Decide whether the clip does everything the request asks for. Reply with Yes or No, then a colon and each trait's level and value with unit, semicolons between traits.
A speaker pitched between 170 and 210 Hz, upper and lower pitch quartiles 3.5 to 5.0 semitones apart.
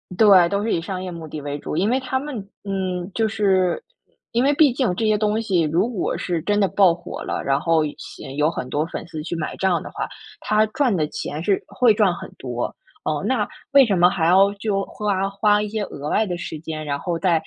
Yes: high, 190 Hz; average, 4.3 semitones